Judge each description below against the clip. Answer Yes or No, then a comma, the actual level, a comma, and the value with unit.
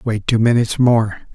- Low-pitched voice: Yes, low, 115 Hz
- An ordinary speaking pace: Yes, average, 180 wpm